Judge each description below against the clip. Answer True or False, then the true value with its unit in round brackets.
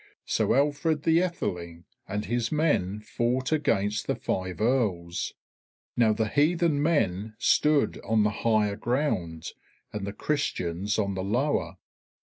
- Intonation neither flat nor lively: False (6.6 semitones)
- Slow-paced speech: True (130 wpm)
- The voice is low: True (110 Hz)